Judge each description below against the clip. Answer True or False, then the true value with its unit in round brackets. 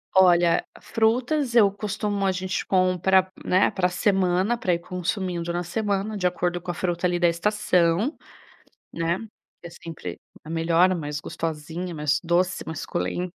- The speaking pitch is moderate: True (180 Hz)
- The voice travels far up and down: False (2.5 semitones)